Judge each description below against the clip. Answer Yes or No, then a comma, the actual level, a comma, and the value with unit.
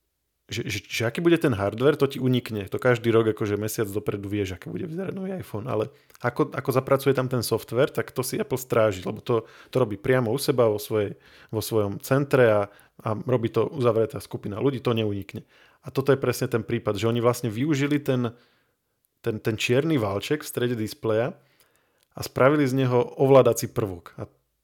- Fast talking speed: Yes, fast, 195 wpm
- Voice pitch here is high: No, low, 120 Hz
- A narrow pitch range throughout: No, average, 3.7 semitones